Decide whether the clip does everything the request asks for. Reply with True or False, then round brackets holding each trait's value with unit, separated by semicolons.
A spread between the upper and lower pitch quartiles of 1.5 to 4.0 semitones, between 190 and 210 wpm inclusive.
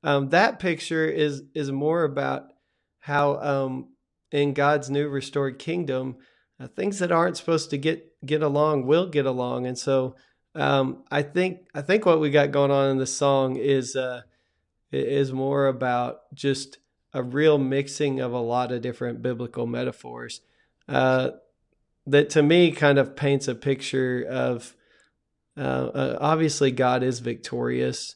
False (2.8 semitones; 155 wpm)